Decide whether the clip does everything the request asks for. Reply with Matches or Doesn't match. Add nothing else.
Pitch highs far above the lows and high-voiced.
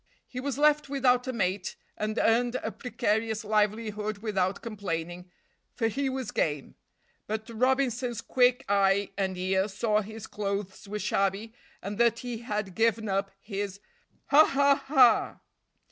Doesn't match